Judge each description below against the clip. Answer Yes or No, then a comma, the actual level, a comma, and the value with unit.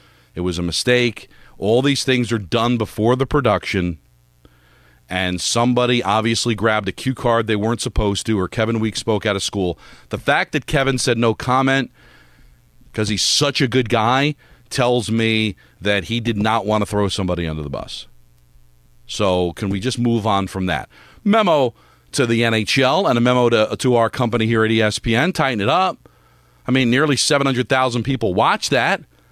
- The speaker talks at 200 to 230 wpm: No, average, 180 wpm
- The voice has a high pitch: No, low, 110 Hz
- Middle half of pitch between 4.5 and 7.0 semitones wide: Yes, average, 4.9 semitones